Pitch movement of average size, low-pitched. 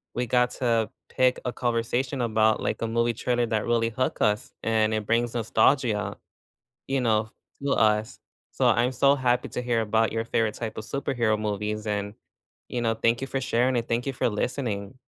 No: narrow, 2.2 semitones; low, 115 Hz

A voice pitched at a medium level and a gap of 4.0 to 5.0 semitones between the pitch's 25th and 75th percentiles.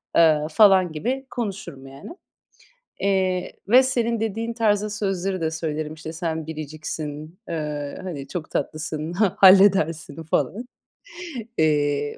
Yes: medium, 165 Hz; average, 4.6 semitones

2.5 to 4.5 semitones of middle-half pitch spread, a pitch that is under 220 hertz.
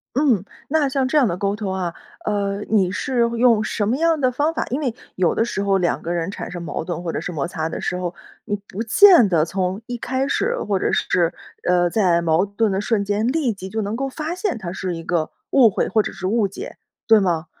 No: wide, 5.6 semitones; high, 205 Hz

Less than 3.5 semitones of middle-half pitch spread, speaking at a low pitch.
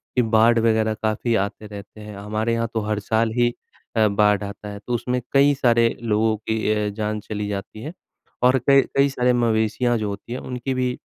Yes: narrow, 2.4 semitones; low, 110 Hz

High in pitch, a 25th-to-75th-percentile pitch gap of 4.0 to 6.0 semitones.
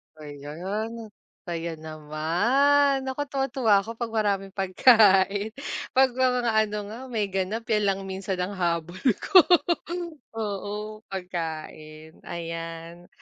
Yes: high, 195 Hz; average, 5.1 semitones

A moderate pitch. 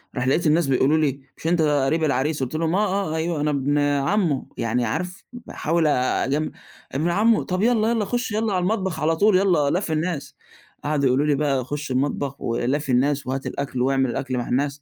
Yes: medium, 150 Hz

